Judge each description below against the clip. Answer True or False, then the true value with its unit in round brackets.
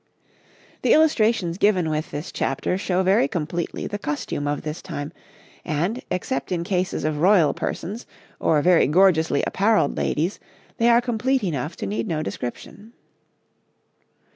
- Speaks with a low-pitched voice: False (175 Hz)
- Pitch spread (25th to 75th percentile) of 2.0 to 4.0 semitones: False (5.1 semitones)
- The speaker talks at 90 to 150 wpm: True (145 wpm)